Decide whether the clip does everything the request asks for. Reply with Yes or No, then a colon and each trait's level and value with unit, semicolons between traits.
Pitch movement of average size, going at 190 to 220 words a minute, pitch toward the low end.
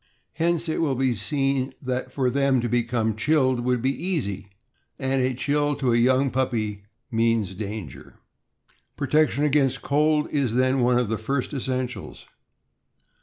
No: average, 3.1 semitones; average, 155 wpm; low, 130 Hz